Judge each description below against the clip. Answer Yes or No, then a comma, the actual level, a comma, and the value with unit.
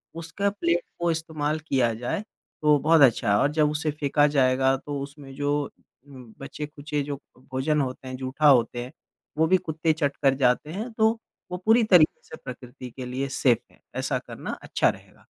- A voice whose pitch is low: No, medium, 145 Hz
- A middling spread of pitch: Yes, average, 3.4 semitones